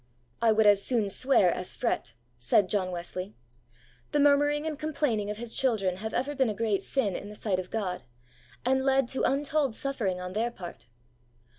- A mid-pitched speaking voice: No, high, 220 Hz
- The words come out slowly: No, average, 190 wpm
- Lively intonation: Yes, wide, 5.8 semitones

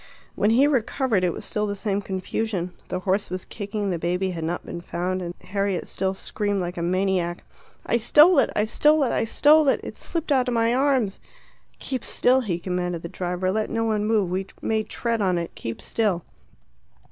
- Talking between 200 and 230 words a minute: Yes, fast, 205 wpm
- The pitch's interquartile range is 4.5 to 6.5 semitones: No, average, 4.1 semitones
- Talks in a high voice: Yes, high, 200 Hz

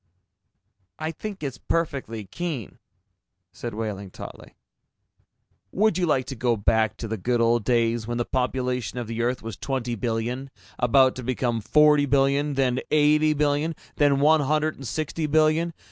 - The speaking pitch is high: No, low, 130 Hz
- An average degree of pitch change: Yes, average, 4.4 semitones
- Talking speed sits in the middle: Yes, average, 160 wpm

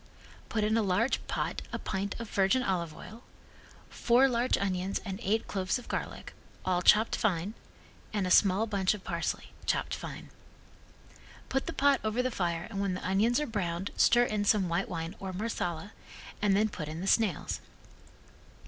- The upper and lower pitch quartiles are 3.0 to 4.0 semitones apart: Yes, average, 3.5 semitones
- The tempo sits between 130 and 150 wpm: No, average, 175 wpm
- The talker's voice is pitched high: Yes, high, 200 Hz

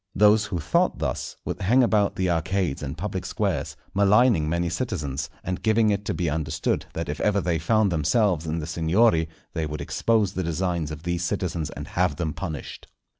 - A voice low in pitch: Yes, very low, 90 Hz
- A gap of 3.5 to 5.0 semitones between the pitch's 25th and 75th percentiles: Yes, average, 4.2 semitones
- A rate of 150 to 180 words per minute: No, average, 190 wpm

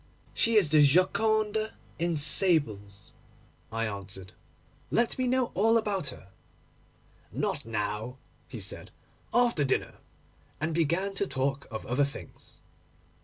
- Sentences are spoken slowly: Yes, slow, 120 wpm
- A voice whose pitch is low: No, medium, 155 Hz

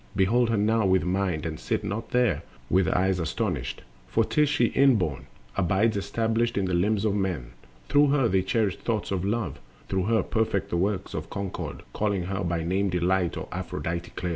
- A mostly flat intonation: No, average, 3.8 semitones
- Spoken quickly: No, average, 190 wpm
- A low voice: Yes, low, 100 Hz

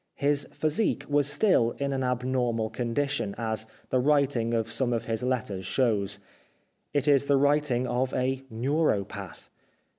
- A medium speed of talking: Yes, average, 150 wpm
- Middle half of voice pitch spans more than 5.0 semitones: No, average, 3.7 semitones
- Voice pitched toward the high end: No, low, 125 Hz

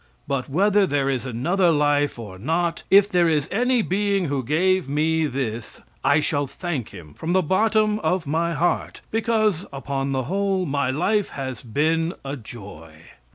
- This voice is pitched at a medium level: Yes, medium, 155 Hz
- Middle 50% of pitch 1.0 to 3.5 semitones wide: No, wide, 5.6 semitones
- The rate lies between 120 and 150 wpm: No, average, 165 wpm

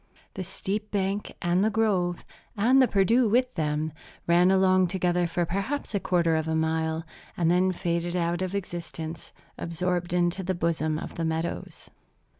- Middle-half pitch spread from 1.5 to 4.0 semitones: Yes, narrow, 2.4 semitones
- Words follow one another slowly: No, average, 165 wpm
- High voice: No, medium, 175 Hz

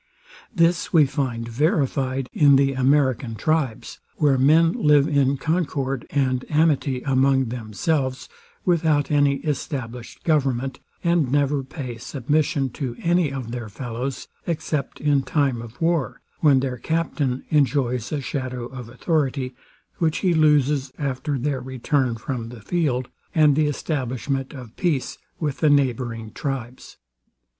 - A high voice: No, low, 135 Hz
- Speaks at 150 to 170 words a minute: No, slow, 135 wpm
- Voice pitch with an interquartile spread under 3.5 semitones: Yes, average, 2.9 semitones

